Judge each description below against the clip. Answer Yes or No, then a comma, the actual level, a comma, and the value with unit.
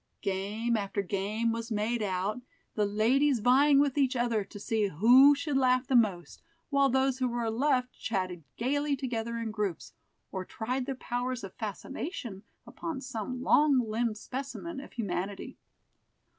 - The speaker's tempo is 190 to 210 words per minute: No, average, 155 wpm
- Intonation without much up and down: No, average, 4.0 semitones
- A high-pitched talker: Yes, high, 235 Hz